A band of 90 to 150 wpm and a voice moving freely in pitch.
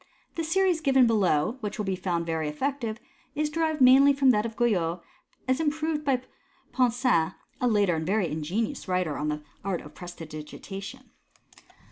No: average, 165 wpm; wide, 7.6 semitones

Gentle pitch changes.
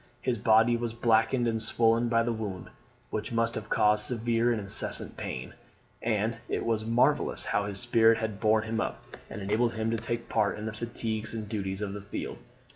Yes: narrow, 1.5 semitones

